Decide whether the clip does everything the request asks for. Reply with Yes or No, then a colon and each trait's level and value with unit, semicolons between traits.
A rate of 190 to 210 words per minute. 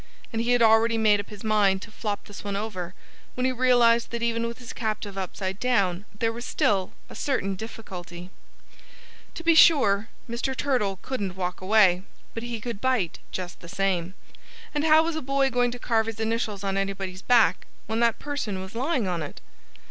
Yes: average, 195 wpm